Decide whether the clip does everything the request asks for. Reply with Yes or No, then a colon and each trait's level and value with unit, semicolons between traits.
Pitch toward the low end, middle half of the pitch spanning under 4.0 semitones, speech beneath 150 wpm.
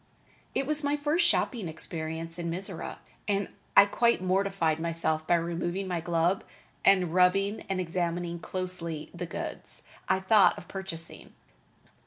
No: medium, 180 Hz; average, 2.9 semitones; average, 140 wpm